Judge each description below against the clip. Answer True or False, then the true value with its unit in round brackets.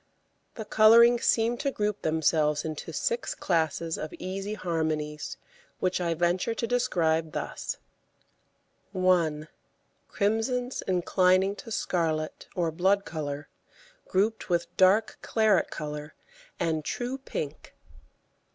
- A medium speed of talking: False (110 wpm)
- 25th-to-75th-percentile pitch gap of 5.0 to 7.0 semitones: True (5.4 semitones)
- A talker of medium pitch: True (180 Hz)